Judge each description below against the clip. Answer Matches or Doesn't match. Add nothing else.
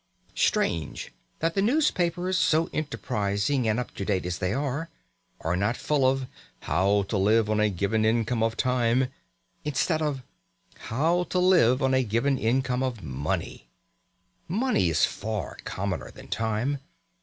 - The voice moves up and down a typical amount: Doesn't match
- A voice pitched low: Matches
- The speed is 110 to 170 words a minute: Matches